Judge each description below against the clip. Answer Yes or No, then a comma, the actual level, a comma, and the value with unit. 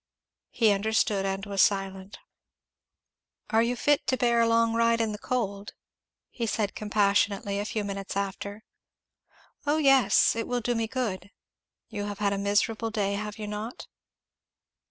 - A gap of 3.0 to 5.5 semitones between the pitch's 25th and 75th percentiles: No, narrow, 2.4 semitones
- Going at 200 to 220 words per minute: No, average, 155 wpm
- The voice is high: Yes, high, 210 Hz